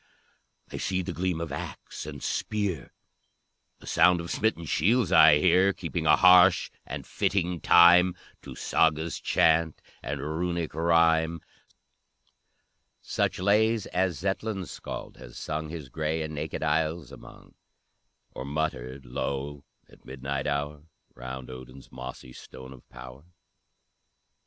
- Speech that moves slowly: Yes, slow, 130 wpm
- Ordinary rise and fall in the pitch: Yes, average, 4.1 semitones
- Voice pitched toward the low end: Yes, very low, 80 Hz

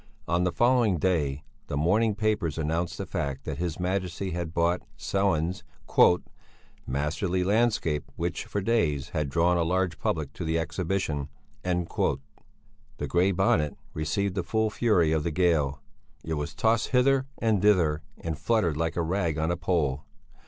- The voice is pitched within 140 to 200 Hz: No, very low, 85 Hz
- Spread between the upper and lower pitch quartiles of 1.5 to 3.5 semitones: No, average, 3.9 semitones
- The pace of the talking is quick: No, average, 155 wpm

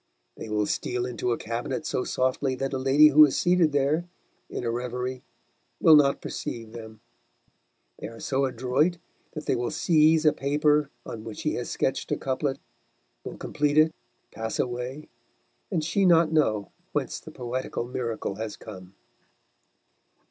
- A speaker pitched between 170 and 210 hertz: No, low, 130 Hz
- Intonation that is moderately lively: Yes, average, 4.3 semitones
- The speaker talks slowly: No, average, 160 wpm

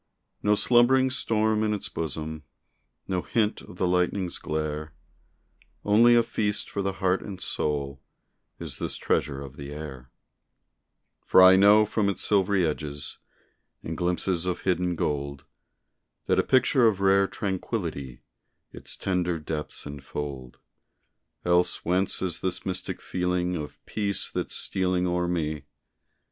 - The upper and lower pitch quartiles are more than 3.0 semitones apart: Yes, average, 4.5 semitones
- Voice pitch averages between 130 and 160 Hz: No, very low, 90 Hz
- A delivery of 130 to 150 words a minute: Yes, slow, 135 wpm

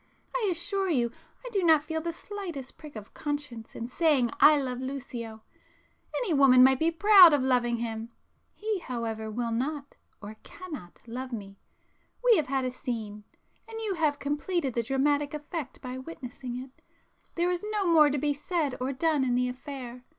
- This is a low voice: No, very high, 275 Hz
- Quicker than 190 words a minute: No, average, 165 wpm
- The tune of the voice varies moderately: Yes, average, 4.9 semitones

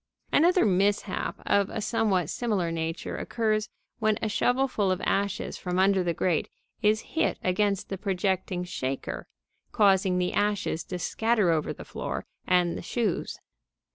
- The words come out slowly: No, average, 145 wpm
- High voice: Yes, high, 195 Hz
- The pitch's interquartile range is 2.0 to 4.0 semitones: Yes, average, 3.0 semitones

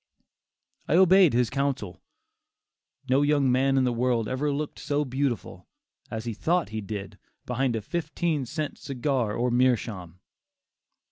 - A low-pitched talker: Yes, low, 130 Hz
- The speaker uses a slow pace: No, average, 145 wpm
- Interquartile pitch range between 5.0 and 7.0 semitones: No, average, 3.8 semitones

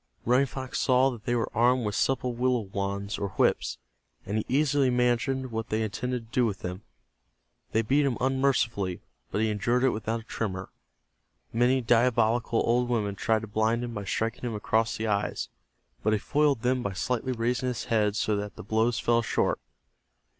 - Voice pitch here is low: Yes, low, 115 Hz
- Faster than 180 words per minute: Yes, average, 190 wpm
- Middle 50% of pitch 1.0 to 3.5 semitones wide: Yes, average, 2.7 semitones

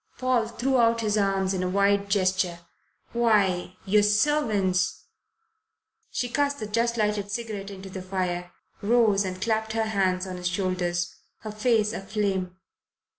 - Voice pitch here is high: Yes, high, 205 Hz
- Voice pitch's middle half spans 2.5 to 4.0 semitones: Yes, average, 3.2 semitones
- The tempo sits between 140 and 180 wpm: Yes, average, 150 wpm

